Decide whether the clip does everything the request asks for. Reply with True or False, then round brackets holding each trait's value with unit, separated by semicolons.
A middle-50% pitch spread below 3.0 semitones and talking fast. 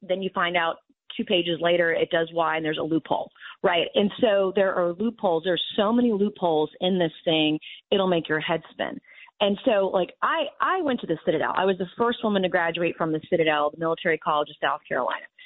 False (3.6 semitones; 220 wpm)